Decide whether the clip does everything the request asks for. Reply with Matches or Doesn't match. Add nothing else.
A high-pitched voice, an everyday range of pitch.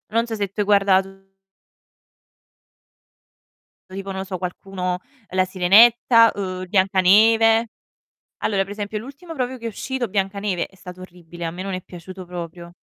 Matches